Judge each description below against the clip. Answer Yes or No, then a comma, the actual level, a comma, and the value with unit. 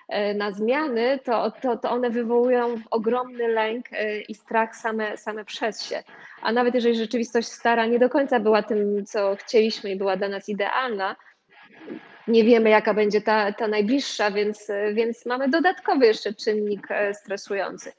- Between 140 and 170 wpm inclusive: Yes, average, 155 wpm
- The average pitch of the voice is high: Yes, high, 225 Hz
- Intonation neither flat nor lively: No, narrow, 2.3 semitones